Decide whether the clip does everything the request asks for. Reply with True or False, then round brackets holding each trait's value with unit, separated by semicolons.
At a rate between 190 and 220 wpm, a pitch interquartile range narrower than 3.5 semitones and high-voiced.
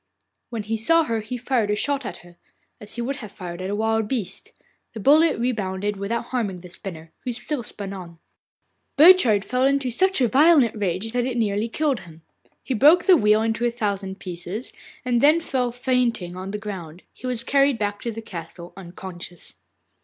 False (195 wpm; 4.7 semitones; 225 Hz)